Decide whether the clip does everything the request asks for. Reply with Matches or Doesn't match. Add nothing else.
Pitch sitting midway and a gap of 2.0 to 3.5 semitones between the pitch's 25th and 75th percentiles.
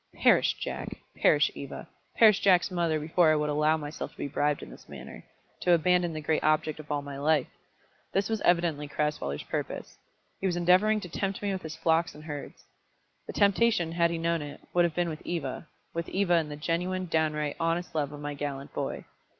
Matches